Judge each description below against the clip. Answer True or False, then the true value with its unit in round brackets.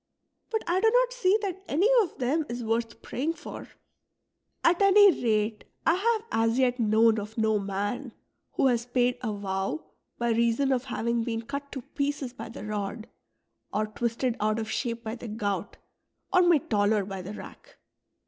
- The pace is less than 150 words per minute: False (175 wpm)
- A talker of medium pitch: False (235 Hz)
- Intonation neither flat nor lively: True (4.9 semitones)